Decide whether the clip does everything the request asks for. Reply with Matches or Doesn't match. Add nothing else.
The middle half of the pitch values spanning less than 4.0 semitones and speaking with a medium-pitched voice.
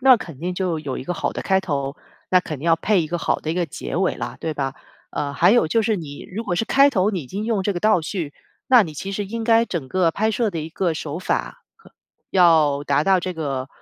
Doesn't match